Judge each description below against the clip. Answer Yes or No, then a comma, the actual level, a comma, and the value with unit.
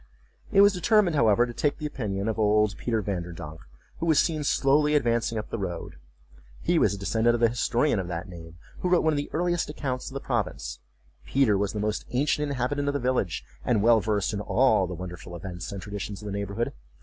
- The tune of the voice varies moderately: No, wide, 6.1 semitones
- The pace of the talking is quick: Yes, fast, 220 wpm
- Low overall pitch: Yes, low, 115 Hz